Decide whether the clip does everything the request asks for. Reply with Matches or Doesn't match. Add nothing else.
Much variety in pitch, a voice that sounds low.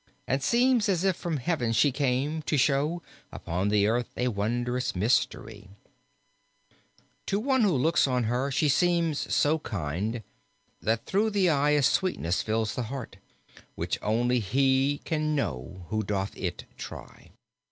Matches